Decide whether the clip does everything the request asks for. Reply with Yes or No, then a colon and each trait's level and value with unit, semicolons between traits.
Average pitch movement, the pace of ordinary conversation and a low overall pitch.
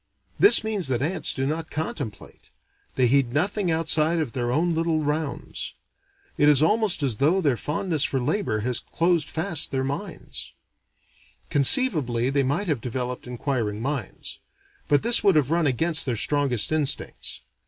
No: average, 4.4 semitones; average, 155 wpm; medium, 145 Hz